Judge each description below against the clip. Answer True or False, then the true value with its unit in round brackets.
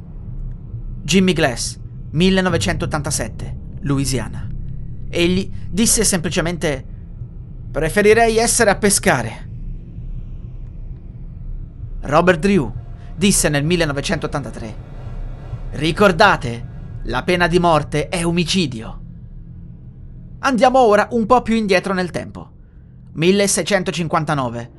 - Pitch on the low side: False (155 Hz)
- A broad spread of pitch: True (7.3 semitones)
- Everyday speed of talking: False (75 wpm)